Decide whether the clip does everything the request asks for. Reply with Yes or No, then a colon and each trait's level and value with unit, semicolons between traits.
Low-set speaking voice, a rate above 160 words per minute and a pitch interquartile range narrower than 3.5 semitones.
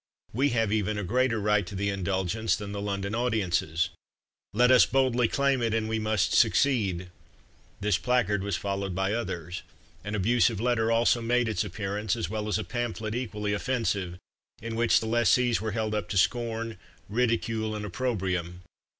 Yes: low, 110 Hz; average, 170 wpm; average, 3.0 semitones